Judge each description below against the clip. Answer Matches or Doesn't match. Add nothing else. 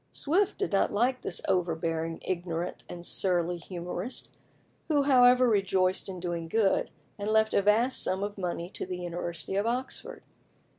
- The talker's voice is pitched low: Doesn't match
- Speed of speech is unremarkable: Matches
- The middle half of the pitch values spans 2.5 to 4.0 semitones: Doesn't match